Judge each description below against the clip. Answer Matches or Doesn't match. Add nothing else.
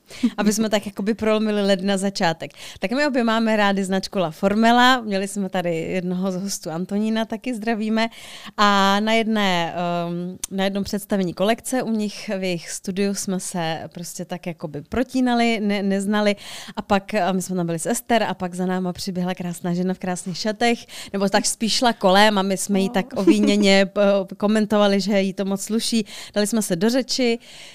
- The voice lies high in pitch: Matches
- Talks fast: Matches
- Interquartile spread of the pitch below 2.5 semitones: Doesn't match